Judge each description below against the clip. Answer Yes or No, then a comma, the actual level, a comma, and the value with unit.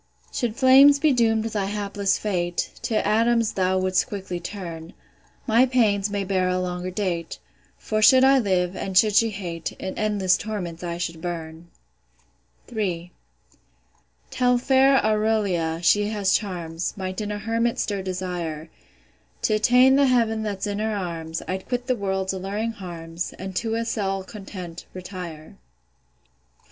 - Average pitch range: Yes, average, 3.7 semitones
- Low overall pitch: No, high, 195 Hz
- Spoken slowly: No, average, 155 wpm